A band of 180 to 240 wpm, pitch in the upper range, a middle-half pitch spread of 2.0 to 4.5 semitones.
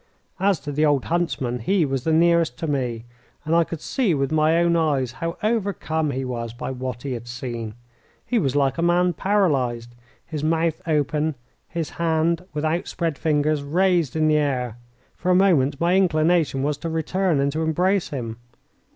No: average, 185 wpm; medium, 155 Hz; average, 4.0 semitones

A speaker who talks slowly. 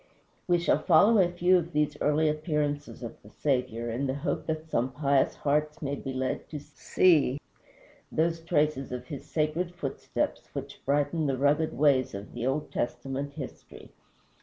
No: average, 165 wpm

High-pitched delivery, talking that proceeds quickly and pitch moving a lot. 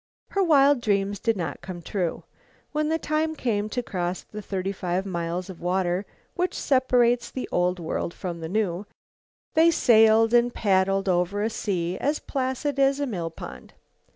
No: high, 205 Hz; average, 170 wpm; wide, 6.1 semitones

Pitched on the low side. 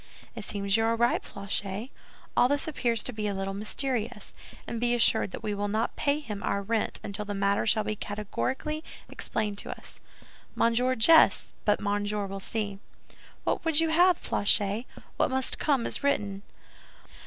No: high, 215 Hz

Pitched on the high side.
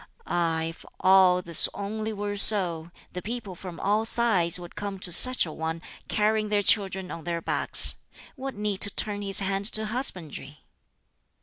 Yes: high, 195 Hz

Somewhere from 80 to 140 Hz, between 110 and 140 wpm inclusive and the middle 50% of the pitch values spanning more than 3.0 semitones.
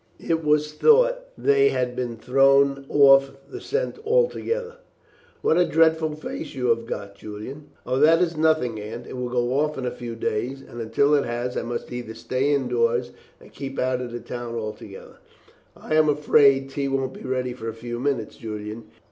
No: low, 135 Hz; average, 190 wpm; average, 4.2 semitones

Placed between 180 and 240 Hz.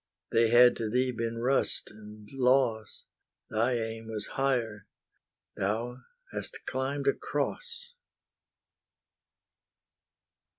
No: low, 120 Hz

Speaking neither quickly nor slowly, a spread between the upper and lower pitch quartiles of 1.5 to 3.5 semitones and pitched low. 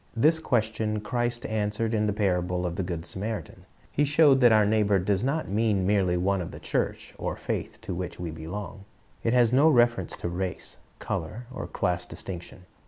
No: average, 185 wpm; average, 4.4 semitones; low, 105 Hz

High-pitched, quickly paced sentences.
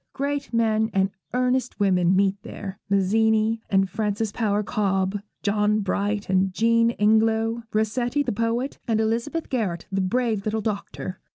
No: high, 215 Hz; average, 145 wpm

